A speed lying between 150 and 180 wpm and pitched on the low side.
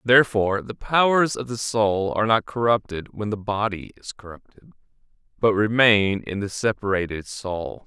Yes: average, 155 wpm; low, 105 Hz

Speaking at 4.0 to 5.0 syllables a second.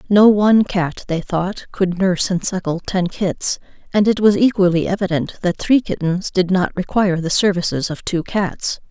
Yes: 4.7 syllables/s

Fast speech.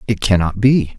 No: average, 185 wpm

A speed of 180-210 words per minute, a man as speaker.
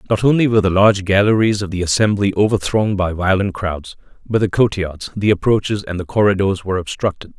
Yes: average, 185 wpm; male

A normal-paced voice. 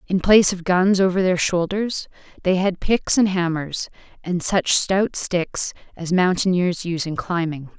Yes: average, 160 wpm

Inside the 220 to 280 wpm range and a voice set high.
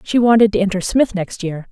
Yes: fast, 245 wpm; high, 200 Hz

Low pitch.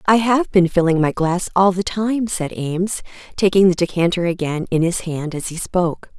No: medium, 180 Hz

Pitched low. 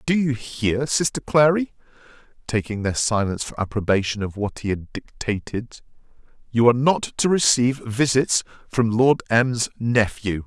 Yes: low, 120 Hz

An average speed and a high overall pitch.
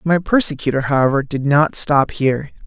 No: average, 160 wpm; medium, 145 Hz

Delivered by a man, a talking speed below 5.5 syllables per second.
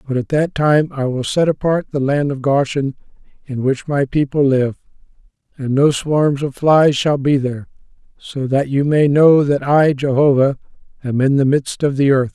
Yes: male; 4.7 syllables/s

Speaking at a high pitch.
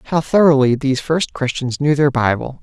No: medium, 140 Hz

